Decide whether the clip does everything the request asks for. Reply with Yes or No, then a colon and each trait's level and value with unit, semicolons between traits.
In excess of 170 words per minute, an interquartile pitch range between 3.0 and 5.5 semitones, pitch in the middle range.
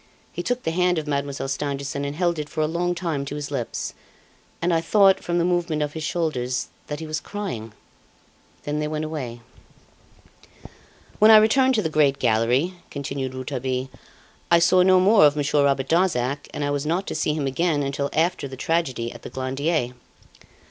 Yes: average, 190 wpm; average, 4.0 semitones; medium, 150 Hz